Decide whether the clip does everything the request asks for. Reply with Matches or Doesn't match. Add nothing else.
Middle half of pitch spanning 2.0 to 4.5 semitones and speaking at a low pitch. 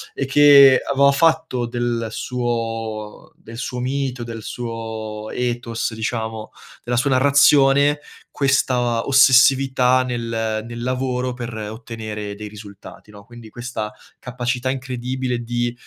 Matches